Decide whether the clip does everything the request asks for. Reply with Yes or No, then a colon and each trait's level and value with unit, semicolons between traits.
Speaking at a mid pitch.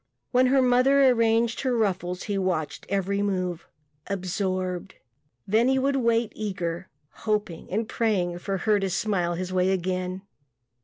No: high, 195 Hz